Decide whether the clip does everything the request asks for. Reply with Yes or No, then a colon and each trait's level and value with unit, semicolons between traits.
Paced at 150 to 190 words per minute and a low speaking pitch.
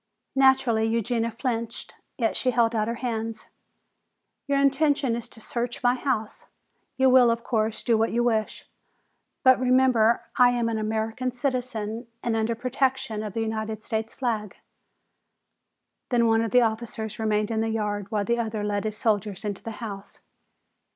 No: average, 170 wpm; high, 230 Hz